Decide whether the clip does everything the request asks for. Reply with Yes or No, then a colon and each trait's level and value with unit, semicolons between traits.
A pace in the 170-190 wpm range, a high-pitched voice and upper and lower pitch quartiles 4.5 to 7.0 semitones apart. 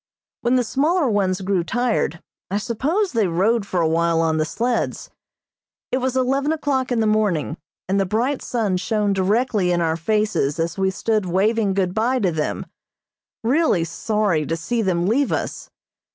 Yes: average, 175 wpm; high, 210 Hz; average, 5.3 semitones